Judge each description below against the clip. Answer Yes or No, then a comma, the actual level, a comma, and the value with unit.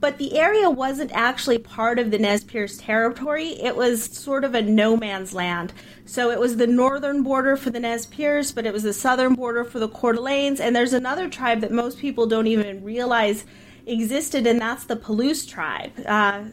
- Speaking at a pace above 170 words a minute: Yes, fast, 205 wpm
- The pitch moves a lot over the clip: No, average, 3.0 semitones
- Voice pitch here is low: No, high, 240 Hz